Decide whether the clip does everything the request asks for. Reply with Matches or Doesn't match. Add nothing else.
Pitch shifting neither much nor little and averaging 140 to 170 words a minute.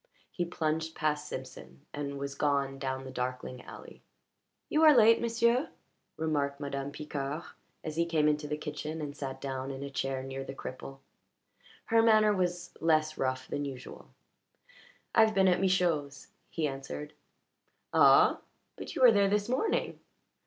Matches